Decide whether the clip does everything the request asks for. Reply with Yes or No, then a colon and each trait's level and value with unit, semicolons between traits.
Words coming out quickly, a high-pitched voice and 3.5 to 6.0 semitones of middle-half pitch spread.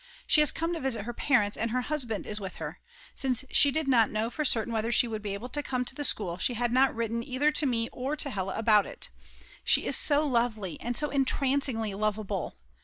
Yes: fast, 235 wpm; high, 240 Hz; average, 4.1 semitones